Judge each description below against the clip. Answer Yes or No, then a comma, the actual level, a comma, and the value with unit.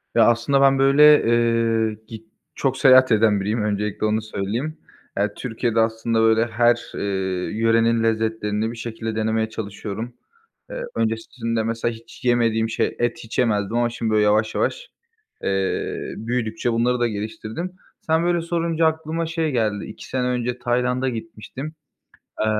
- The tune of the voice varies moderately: No, narrow, 2.2 semitones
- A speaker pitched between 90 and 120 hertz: Yes, low, 115 Hz